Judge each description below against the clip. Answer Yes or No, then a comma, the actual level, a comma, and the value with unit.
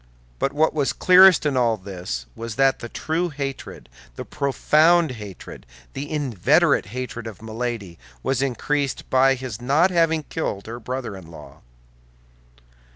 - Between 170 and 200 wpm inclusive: No, average, 145 wpm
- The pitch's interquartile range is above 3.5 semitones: Yes, average, 5.1 semitones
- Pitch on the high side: No, low, 130 Hz